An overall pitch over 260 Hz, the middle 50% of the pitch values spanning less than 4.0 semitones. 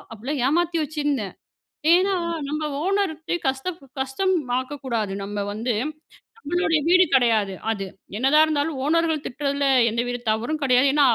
No: very high, 285 Hz; average, 4.7 semitones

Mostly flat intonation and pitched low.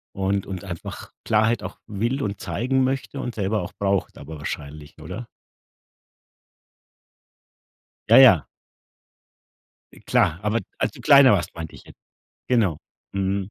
No: average, 4.1 semitones; low, 100 Hz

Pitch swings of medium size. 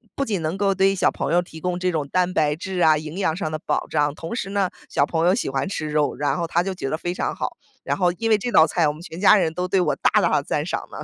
Yes: average, 3.4 semitones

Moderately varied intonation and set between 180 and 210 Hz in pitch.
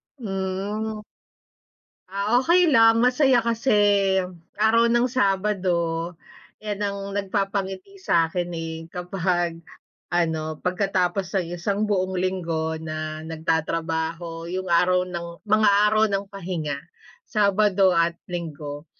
Yes: average, 3.8 semitones; medium, 185 Hz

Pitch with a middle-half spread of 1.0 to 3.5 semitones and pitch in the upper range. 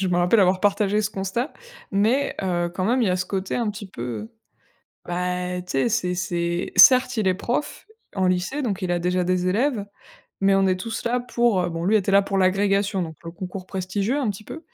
Yes: average, 2.9 semitones; high, 195 Hz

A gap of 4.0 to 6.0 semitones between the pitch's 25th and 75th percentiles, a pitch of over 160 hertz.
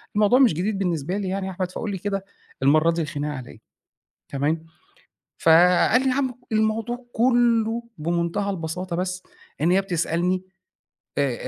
Yes: average, 4.7 semitones; medium, 185 Hz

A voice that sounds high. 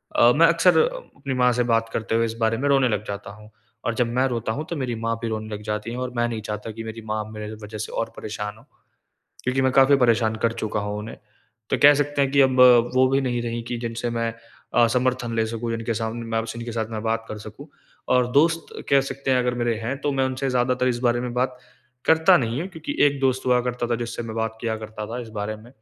No: low, 120 Hz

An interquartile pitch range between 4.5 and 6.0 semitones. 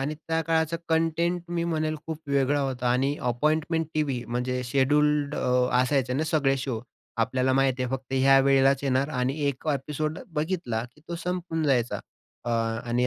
No: average, 3.5 semitones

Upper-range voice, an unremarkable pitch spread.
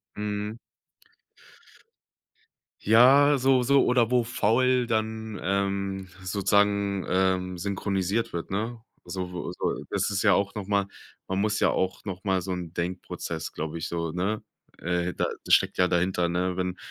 No: low, 100 Hz; average, 3.2 semitones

